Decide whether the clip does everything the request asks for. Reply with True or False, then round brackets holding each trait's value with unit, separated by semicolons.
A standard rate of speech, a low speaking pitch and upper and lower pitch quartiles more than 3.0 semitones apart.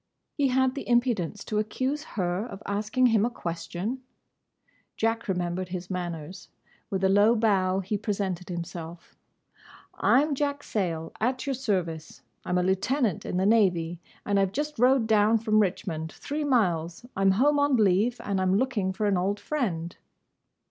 False (170 wpm; 205 Hz; 5.1 semitones)